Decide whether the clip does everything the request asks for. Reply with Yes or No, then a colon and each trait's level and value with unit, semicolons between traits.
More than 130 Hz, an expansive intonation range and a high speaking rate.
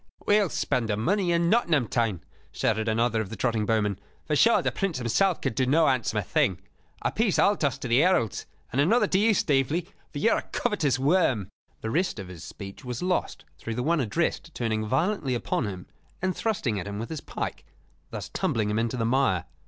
No: low, 125 Hz; wide, 7.7 semitones; fast, 215 wpm